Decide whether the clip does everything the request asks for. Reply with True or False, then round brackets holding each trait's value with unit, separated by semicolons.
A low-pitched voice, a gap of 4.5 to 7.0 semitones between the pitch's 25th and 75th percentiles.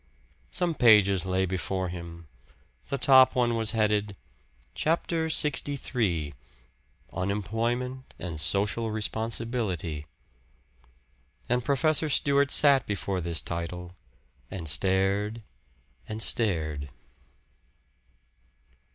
True (105 Hz; 5.5 semitones)